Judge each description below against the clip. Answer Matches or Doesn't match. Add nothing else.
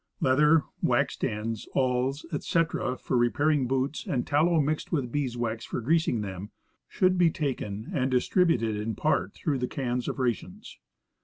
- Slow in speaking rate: Doesn't match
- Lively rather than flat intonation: Doesn't match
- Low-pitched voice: Matches